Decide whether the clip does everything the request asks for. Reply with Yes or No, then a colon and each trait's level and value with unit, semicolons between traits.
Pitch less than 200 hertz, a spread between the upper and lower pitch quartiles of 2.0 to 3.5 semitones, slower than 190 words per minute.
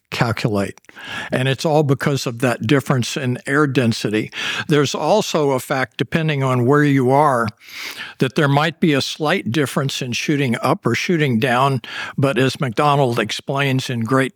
Yes: medium, 140 Hz; average, 2.7 semitones; average, 165 wpm